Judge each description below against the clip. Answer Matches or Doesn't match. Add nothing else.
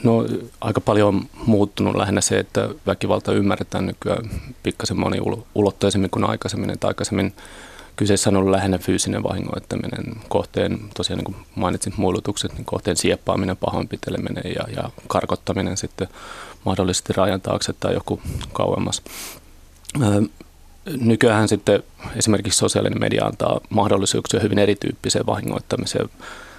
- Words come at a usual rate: Matches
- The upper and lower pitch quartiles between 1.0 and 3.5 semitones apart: Matches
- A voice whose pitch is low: Matches